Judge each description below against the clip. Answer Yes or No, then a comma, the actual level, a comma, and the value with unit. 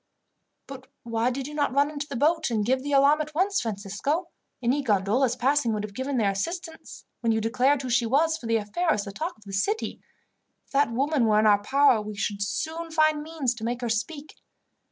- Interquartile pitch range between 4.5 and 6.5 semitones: Yes, average, 5.1 semitones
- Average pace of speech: No, fast, 220 wpm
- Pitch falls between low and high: No, very high, 260 Hz